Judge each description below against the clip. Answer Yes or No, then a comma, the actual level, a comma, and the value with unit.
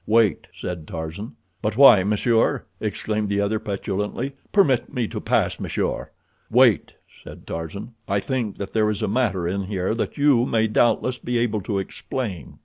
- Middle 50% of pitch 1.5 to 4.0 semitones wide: Yes, average, 3.3 semitones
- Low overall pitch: Yes, low, 105 Hz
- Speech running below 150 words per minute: No, average, 165 wpm